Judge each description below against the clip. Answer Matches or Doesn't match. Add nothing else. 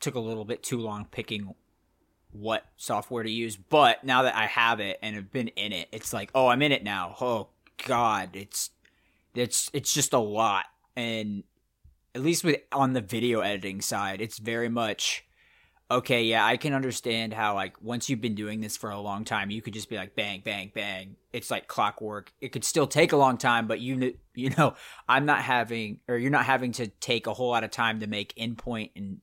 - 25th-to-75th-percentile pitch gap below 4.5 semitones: Matches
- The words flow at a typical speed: Doesn't match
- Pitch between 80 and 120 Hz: Matches